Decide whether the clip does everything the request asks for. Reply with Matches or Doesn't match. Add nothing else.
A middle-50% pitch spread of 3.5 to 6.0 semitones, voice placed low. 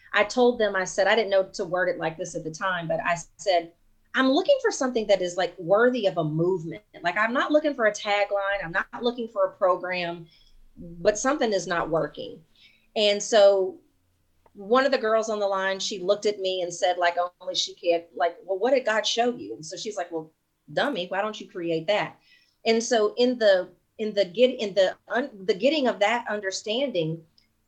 Doesn't match